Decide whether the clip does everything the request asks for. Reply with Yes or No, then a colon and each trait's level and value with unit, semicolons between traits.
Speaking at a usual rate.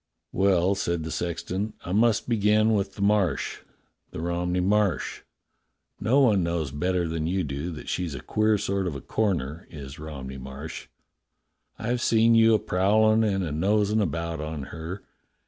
Yes: average, 175 wpm